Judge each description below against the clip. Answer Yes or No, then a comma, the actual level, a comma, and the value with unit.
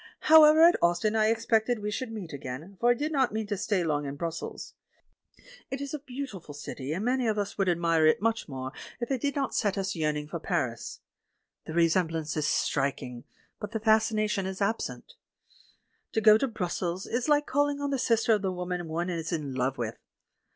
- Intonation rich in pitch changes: Yes, wide, 6.3 semitones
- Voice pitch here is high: Yes, high, 200 Hz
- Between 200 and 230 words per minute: Yes, fast, 205 wpm